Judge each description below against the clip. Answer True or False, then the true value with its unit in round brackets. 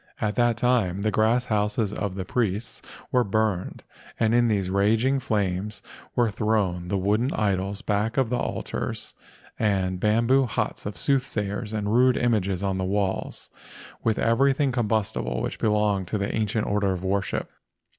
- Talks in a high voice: False (105 Hz)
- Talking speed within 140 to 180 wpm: True (170 wpm)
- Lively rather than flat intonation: False (2.8 semitones)